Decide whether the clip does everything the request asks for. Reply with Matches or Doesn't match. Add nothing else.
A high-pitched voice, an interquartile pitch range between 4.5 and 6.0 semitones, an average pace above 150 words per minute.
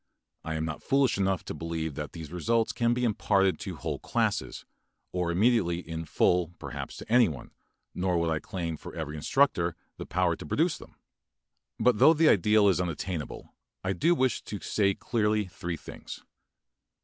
Doesn't match